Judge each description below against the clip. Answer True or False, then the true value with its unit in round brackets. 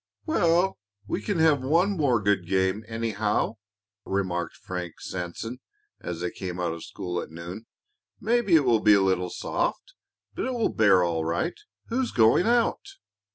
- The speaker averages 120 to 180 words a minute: True (160 wpm)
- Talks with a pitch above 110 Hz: False (105 Hz)